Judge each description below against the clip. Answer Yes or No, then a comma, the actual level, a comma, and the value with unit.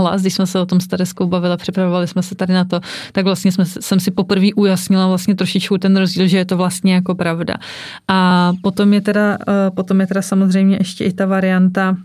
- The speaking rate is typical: No, fast, 215 wpm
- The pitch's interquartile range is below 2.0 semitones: Yes, narrow, 1.1 semitones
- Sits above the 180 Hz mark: Yes, high, 190 Hz